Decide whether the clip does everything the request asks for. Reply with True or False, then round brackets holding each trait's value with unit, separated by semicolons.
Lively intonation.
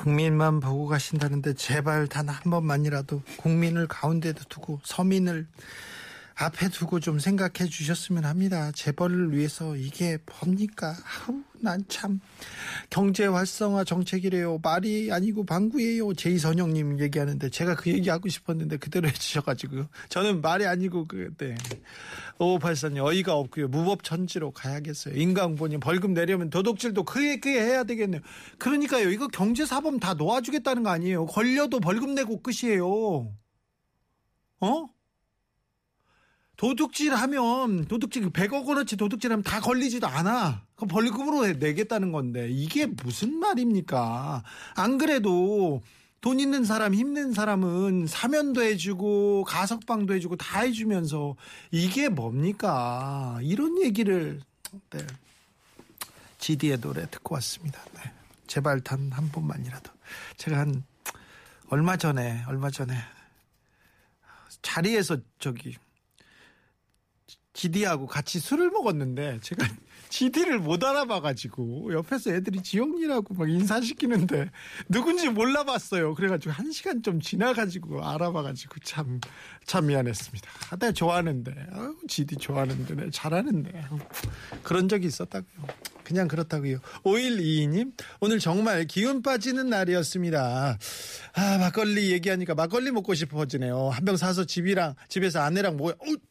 True (6.3 semitones)